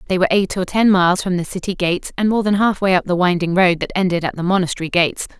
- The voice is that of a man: No, female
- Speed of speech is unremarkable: No, fast, 280 wpm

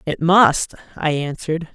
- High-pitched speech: No, medium, 160 Hz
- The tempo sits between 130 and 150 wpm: Yes, slow, 135 wpm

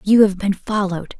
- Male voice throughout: No, female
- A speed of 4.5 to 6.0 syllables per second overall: Yes, 5.5 syllables/s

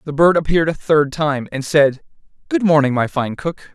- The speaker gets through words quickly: Yes, fast, 210 wpm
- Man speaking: Yes, male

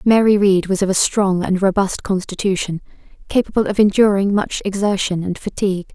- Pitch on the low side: No, high, 195 Hz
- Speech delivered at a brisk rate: No, average, 160 wpm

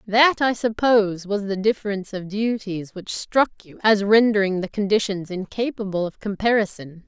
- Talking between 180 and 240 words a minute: No, average, 155 wpm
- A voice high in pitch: Yes, high, 205 Hz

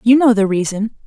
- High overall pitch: Yes, high, 220 Hz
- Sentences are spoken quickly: Yes, fast, 225 wpm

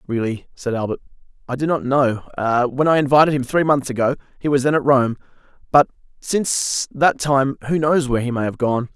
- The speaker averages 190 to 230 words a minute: Yes, average, 200 wpm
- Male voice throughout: Yes, male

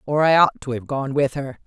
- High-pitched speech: No, low, 135 Hz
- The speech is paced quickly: Yes, fast, 290 wpm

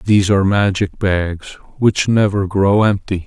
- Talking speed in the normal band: Yes, average, 145 wpm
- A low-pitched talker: Yes, low, 100 Hz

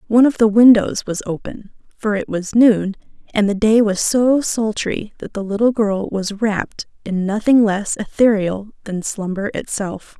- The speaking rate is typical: Yes, average, 170 wpm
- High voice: Yes, high, 210 Hz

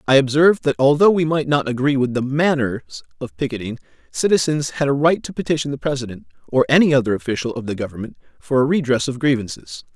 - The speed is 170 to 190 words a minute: No, average, 200 wpm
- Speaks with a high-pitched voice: No, medium, 140 Hz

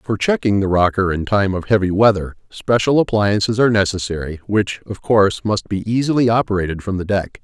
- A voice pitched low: Yes, low, 100 Hz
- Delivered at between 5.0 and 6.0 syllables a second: Yes, 5.6 syllables/s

